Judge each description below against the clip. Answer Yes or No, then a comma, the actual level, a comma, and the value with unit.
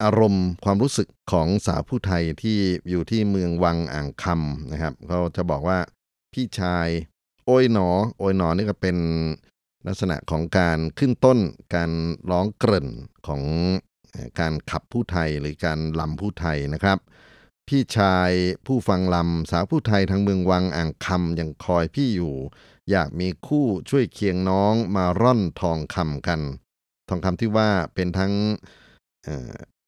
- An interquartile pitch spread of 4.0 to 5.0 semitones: No, average, 3.6 semitones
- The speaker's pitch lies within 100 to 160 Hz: No, very low, 90 Hz